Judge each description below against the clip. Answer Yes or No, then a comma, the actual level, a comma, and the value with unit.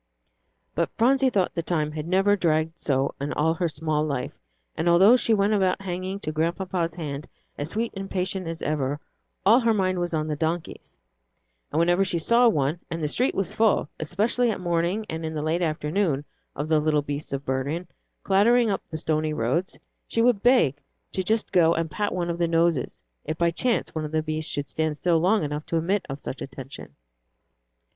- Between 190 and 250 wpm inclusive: Yes, average, 200 wpm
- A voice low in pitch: No, medium, 165 Hz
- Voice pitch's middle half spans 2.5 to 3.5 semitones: No, average, 4.1 semitones